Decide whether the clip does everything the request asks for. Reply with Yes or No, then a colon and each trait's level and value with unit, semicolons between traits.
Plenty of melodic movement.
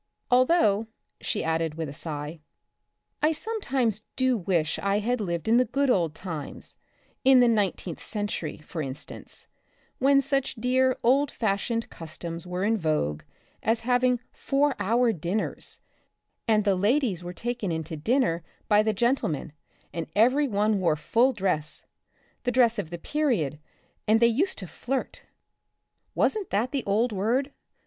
Yes: wide, 6.7 semitones